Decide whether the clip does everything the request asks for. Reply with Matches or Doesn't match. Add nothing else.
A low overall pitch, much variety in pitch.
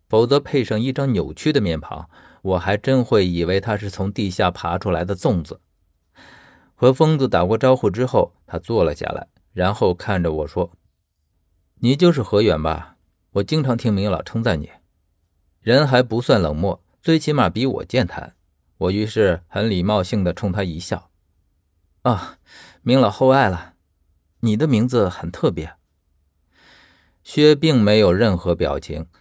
Matches